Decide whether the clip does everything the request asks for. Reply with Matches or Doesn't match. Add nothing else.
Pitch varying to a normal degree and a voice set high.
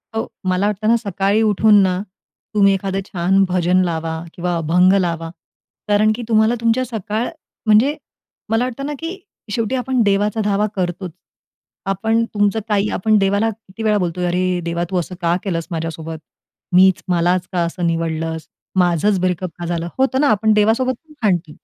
Matches